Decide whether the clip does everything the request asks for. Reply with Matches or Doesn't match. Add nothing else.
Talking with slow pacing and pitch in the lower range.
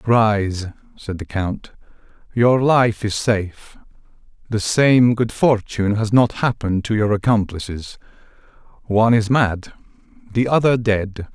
Matches